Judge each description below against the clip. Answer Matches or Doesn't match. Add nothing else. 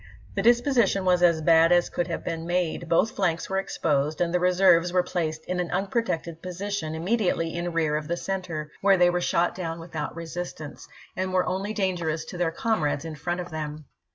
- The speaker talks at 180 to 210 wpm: Matches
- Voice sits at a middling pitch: Matches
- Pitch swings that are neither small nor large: Doesn't match